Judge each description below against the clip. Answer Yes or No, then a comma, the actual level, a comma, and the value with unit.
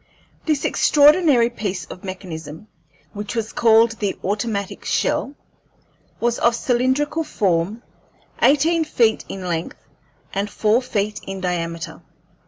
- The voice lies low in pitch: No, high, 220 Hz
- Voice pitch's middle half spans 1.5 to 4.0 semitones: No, average, 4.8 semitones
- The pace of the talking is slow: Yes, slow, 115 wpm